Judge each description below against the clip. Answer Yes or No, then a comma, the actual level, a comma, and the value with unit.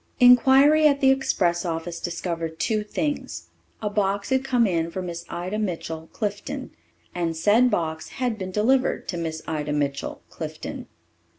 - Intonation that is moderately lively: No, wide, 7.0 semitones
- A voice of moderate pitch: No, high, 195 Hz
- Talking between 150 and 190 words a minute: Yes, average, 155 wpm